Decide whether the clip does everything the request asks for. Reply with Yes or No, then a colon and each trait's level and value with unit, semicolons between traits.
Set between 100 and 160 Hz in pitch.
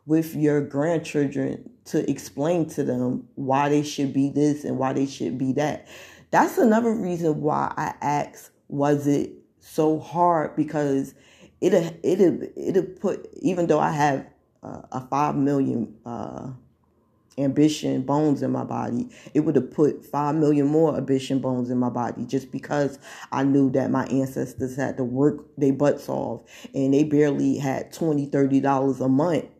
Yes: medium, 140 Hz